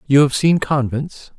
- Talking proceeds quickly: No, average, 175 wpm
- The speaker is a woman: No, male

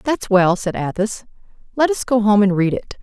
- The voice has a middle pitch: No, high, 210 Hz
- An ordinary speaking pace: No, fast, 220 wpm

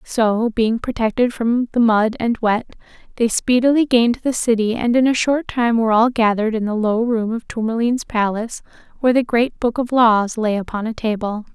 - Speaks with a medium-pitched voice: No, high, 230 Hz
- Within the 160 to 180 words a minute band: No, average, 200 wpm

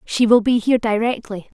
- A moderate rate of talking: Yes, average, 190 wpm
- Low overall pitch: No, high, 225 Hz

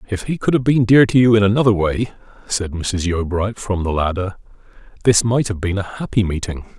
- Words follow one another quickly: Yes, fast, 210 wpm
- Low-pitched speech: Yes, low, 105 Hz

